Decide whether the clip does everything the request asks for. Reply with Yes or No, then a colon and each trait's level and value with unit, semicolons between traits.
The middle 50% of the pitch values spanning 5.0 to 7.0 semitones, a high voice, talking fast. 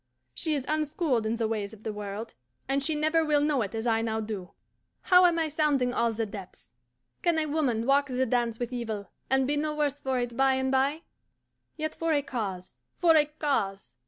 Yes: average, 5.3 semitones; very high, 265 Hz; fast, 215 wpm